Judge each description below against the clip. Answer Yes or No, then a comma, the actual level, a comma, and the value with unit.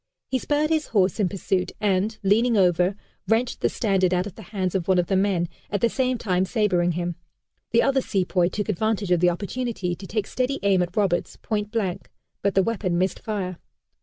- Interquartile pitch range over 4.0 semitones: No, average, 3.5 semitones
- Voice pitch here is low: No, high, 195 Hz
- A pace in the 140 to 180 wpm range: No, fast, 205 wpm